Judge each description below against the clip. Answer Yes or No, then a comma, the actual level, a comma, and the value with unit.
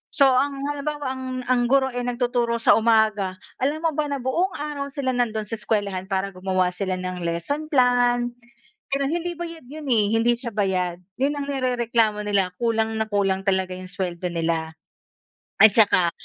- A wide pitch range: Yes, wide, 6.0 semitones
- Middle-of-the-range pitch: No, high, 235 Hz